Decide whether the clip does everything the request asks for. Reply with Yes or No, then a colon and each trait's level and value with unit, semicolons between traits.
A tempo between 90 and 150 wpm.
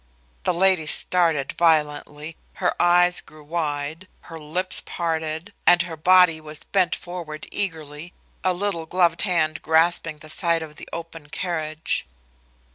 Yes: slow, 135 wpm